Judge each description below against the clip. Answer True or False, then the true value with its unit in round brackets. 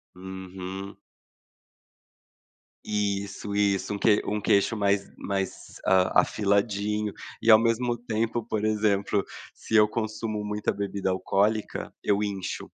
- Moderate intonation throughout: False (1.6 semitones)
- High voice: False (105 Hz)